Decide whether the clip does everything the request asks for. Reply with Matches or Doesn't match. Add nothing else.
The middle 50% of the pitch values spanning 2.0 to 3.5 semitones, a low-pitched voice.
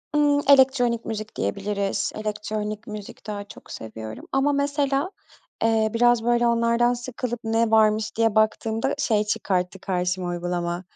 Doesn't match